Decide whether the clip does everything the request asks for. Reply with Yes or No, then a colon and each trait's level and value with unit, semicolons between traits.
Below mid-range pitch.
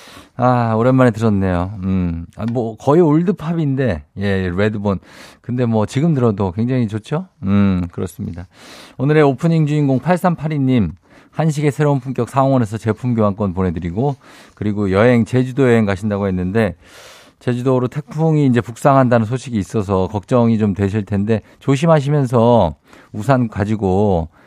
Yes: low, 115 Hz